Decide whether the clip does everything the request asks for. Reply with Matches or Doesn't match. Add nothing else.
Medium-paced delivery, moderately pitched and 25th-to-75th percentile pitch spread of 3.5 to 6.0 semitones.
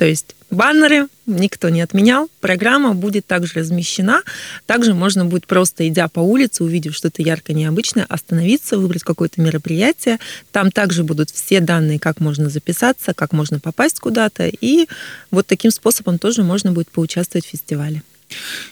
Matches